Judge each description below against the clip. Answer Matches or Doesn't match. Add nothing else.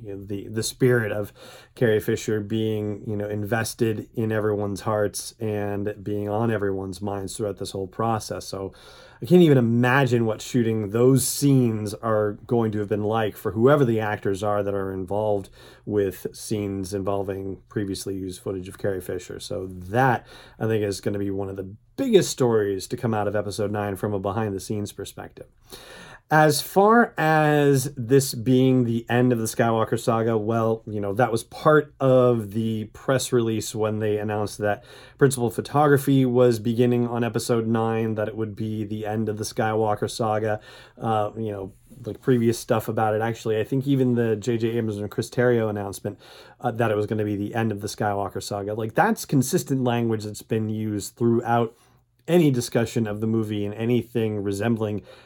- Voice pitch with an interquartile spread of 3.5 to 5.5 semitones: Doesn't match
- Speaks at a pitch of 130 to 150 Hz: Doesn't match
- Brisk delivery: Doesn't match